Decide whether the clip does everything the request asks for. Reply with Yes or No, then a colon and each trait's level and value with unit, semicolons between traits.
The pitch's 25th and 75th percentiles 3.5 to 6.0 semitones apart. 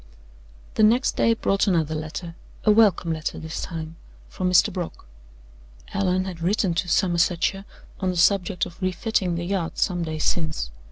No: average, 2.7 semitones